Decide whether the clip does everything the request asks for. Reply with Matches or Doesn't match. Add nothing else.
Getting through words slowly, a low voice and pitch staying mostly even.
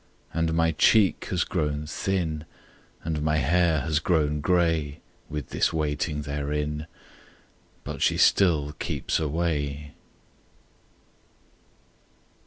Matches